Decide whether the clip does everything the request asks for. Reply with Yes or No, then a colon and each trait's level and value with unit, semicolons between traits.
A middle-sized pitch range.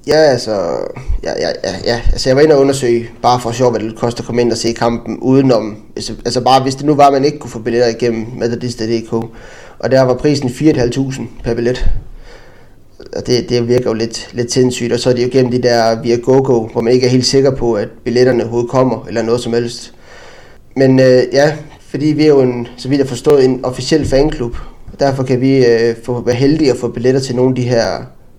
No: narrow, 2.0 semitones